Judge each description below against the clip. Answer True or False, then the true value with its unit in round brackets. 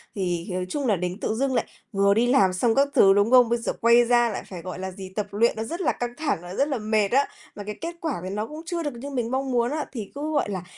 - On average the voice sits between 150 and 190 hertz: False (235 Hz)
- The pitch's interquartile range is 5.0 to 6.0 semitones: True (5.3 semitones)